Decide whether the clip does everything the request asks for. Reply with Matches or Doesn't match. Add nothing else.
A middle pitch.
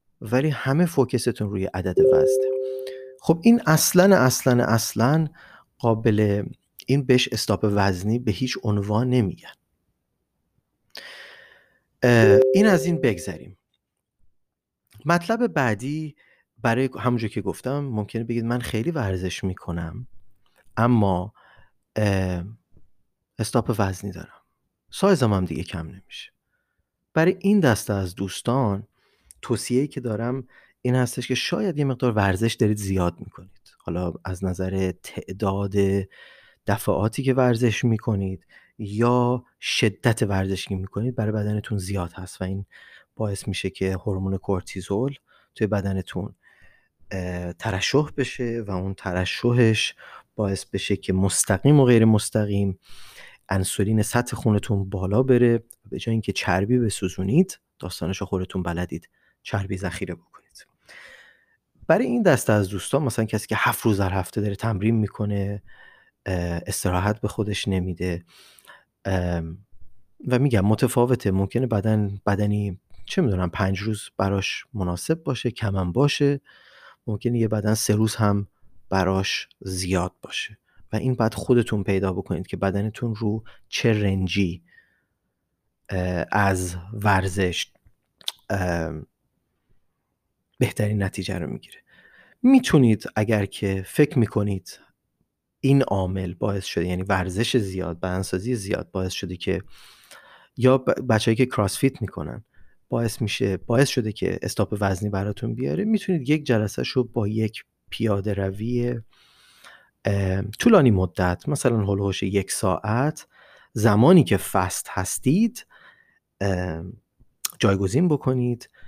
Doesn't match